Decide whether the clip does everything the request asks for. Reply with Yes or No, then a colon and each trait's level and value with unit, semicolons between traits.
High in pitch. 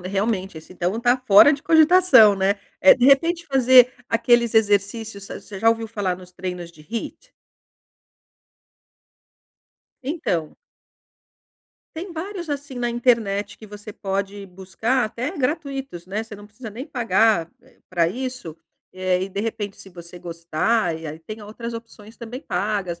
Yes: high, 215 Hz